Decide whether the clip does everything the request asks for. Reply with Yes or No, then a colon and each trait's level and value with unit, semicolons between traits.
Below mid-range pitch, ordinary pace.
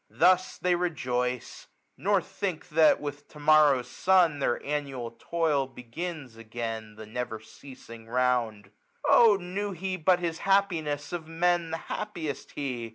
No: medium, 150 Hz; average, 150 wpm